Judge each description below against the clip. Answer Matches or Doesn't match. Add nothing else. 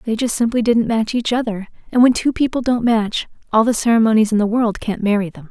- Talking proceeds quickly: Matches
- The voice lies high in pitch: Matches